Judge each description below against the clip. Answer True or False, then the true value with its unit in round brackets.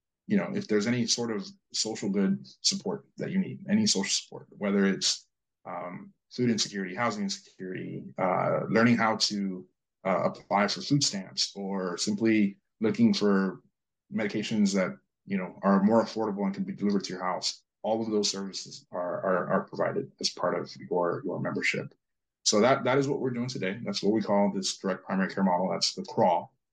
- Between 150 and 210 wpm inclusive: True (190 wpm)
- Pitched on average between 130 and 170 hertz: False (115 Hz)